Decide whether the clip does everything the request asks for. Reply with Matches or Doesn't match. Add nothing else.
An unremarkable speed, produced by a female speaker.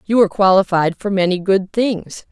Matches